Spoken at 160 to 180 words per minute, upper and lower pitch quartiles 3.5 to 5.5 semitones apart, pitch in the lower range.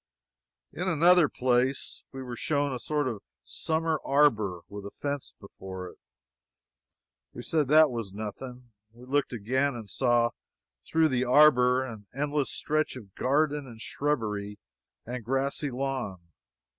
No: average, 140 wpm; average, 4.1 semitones; low, 130 Hz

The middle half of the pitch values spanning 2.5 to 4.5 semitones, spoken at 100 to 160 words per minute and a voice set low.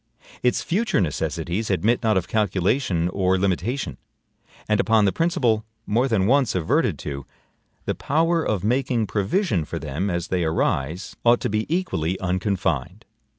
No: average, 5.3 semitones; average, 150 wpm; low, 100 Hz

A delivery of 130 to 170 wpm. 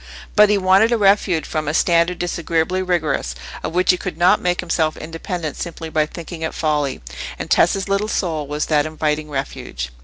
No: average, 185 wpm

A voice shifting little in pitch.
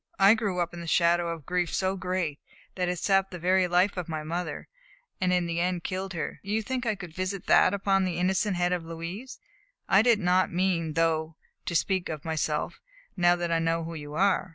Yes: narrow, 2.3 semitones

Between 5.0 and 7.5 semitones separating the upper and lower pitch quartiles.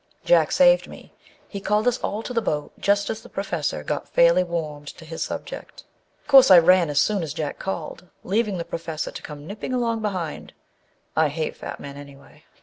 Yes: wide, 5.5 semitones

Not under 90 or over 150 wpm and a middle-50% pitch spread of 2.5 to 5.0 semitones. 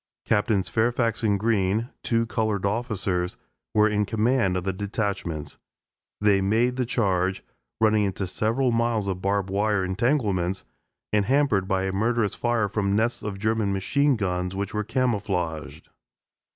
Yes: average, 145 wpm; average, 3.1 semitones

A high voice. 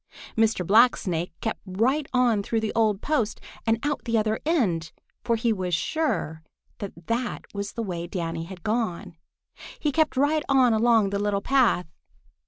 Yes: high, 220 Hz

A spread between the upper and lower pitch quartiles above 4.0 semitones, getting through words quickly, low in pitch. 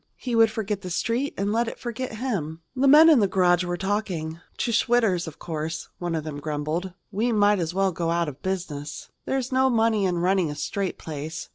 No: wide, 5.6 semitones; fast, 215 wpm; high, 190 Hz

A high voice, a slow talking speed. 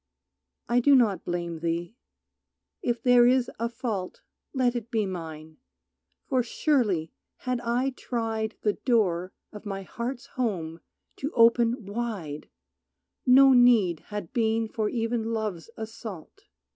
Yes: high, 225 Hz; slow, 130 wpm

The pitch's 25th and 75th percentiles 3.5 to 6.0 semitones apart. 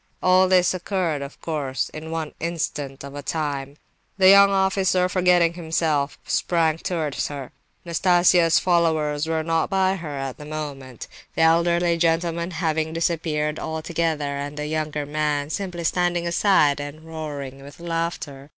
No: average, 2.7 semitones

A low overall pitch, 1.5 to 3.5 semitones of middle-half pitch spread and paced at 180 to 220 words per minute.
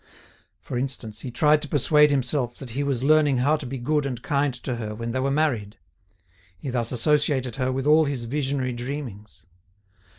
Yes: low, 130 Hz; average, 3.2 semitones; average, 190 wpm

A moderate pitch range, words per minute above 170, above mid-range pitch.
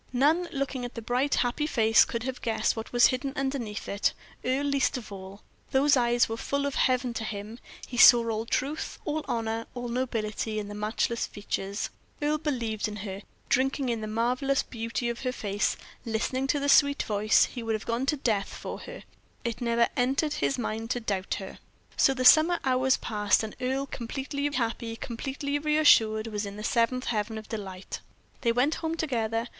Yes: average, 3.5 semitones; average, 190 wpm; high, 240 Hz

